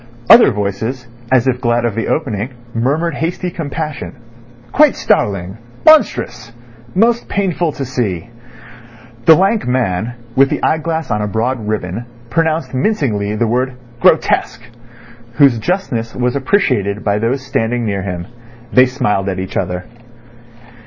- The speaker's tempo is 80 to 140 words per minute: Yes, slow, 135 wpm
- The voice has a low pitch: Yes, low, 125 Hz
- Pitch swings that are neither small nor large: No, wide, 6.5 semitones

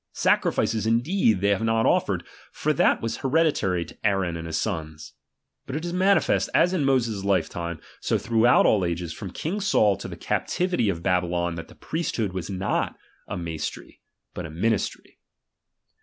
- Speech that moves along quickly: No, average, 175 wpm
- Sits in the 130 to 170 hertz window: No, low, 100 Hz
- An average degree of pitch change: No, wide, 6.3 semitones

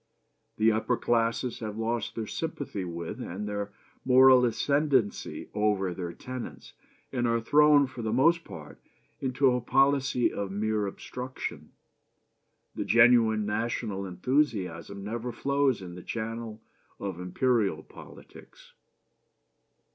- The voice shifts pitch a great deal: No, average, 4.0 semitones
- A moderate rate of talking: No, slow, 120 wpm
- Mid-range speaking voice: No, low, 115 Hz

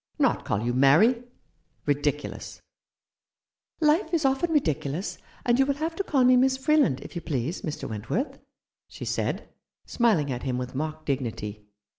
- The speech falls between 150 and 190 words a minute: Yes, average, 170 wpm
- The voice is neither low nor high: Yes, medium, 180 Hz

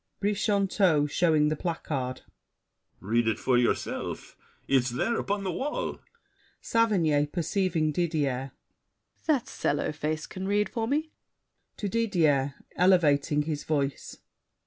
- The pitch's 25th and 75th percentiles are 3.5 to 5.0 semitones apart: No, wide, 5.6 semitones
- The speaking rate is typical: No, slow, 115 wpm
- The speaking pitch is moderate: Yes, medium, 160 Hz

